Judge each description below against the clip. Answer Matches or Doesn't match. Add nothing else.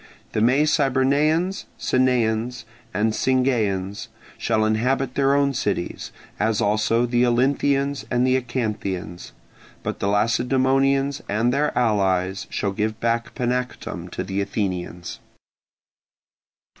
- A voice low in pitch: Matches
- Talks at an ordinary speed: Doesn't match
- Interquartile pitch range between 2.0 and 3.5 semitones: Doesn't match